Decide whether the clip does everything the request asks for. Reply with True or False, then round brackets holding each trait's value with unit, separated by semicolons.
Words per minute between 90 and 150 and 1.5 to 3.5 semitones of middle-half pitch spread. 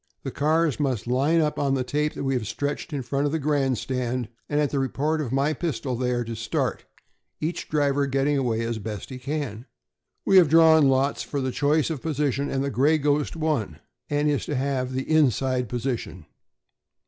False (200 wpm; 2.9 semitones)